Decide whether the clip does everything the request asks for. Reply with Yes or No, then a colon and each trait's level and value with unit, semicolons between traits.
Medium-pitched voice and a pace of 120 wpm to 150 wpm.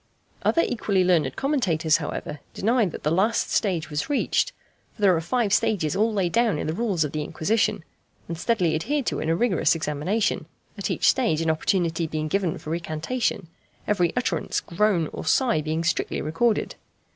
No: medium, 180 Hz; average, 180 wpm